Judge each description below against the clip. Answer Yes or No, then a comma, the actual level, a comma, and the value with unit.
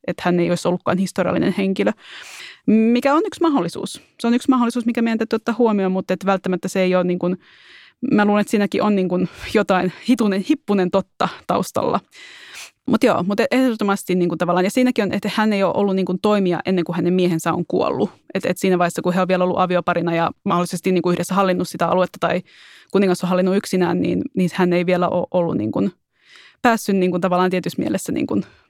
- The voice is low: No, medium, 185 Hz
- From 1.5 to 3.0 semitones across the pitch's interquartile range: Yes, average, 2.7 semitones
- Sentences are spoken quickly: Yes, fast, 215 wpm